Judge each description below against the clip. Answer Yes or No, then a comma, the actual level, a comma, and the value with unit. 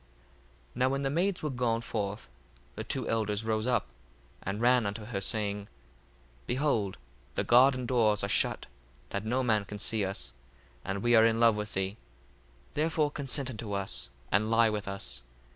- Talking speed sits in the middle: Yes, average, 175 wpm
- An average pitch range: Yes, average, 3.5 semitones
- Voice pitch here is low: Yes, low, 110 Hz